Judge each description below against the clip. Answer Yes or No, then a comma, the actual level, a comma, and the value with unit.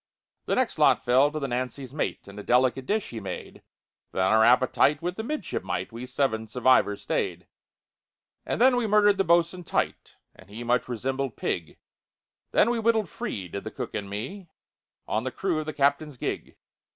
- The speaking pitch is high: No, low, 130 Hz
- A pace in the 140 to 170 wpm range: No, average, 185 wpm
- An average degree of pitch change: No, wide, 7.0 semitones